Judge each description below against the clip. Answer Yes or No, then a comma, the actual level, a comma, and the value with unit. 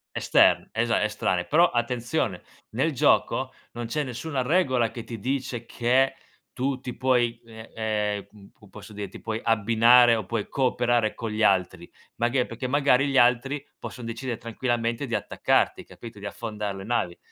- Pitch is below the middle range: Yes, low, 115 Hz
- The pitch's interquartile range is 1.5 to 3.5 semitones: Yes, average, 2.7 semitones